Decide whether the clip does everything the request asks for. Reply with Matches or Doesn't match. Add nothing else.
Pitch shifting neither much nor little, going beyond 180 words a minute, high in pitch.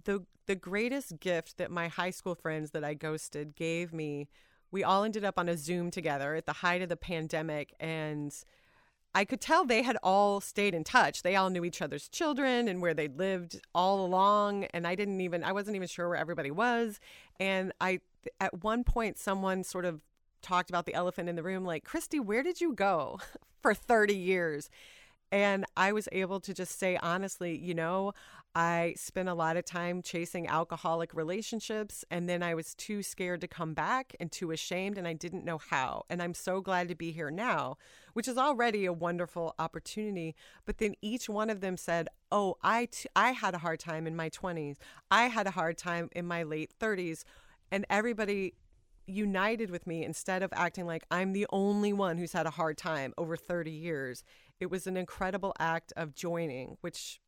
Doesn't match